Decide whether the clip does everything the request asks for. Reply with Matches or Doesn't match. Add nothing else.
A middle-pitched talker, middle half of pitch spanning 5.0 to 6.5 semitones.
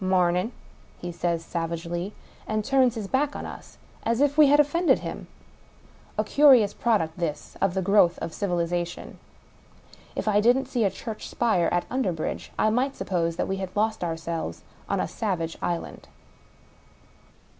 Doesn't match